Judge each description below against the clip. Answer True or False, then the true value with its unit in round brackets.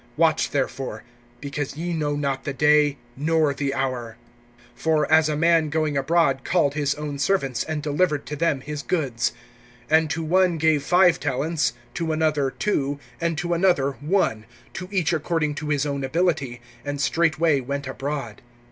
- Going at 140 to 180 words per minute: True (165 wpm)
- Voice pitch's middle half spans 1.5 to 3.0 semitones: True (2.7 semitones)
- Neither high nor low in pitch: True (150 Hz)